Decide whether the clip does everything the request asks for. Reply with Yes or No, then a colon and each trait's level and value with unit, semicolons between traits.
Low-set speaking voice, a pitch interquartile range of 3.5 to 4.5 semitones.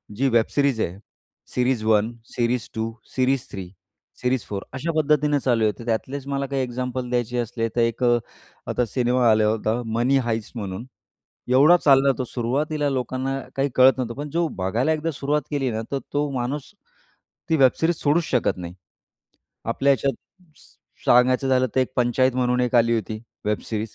No: low, 125 Hz; average, 3.0 semitones